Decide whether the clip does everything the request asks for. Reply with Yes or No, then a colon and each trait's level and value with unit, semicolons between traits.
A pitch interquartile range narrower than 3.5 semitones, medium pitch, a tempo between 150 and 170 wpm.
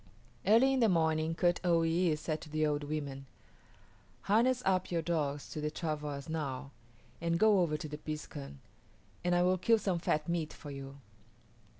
No: average, 3.0 semitones; medium, 160 Hz; average, 180 wpm